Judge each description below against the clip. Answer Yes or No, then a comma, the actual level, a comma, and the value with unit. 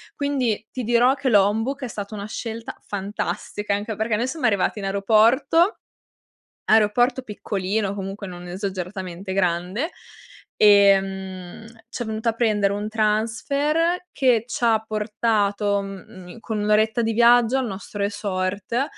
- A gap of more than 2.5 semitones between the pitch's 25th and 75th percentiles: Yes, average, 2.9 semitones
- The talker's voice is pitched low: No, high, 215 Hz